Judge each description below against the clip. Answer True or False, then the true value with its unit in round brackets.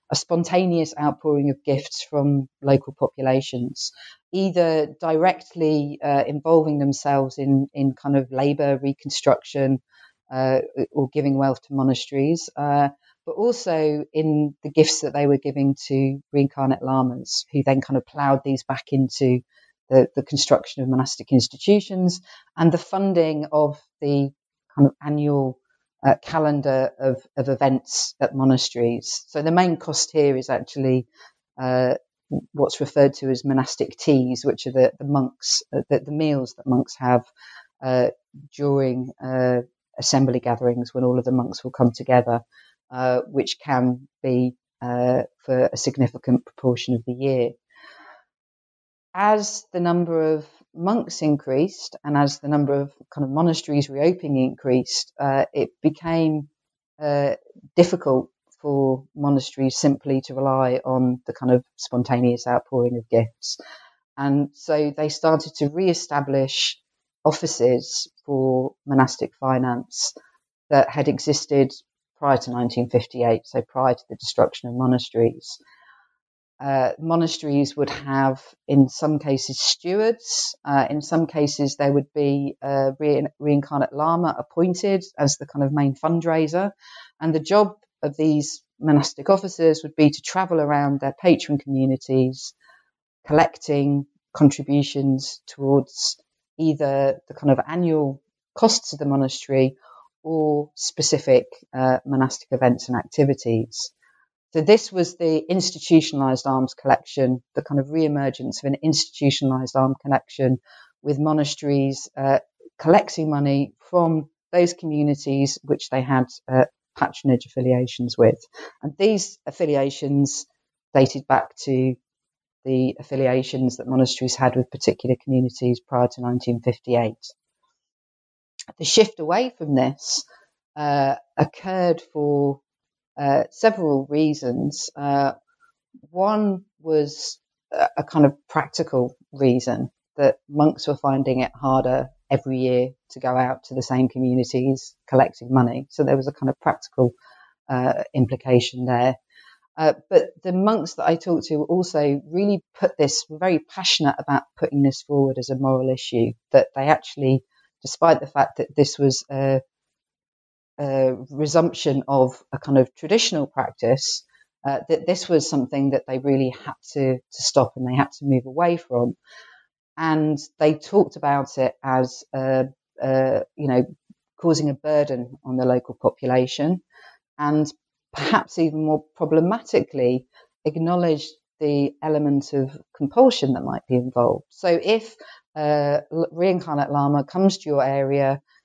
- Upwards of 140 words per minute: False (135 wpm)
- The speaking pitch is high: False (140 Hz)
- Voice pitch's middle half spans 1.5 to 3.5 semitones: True (2.9 semitones)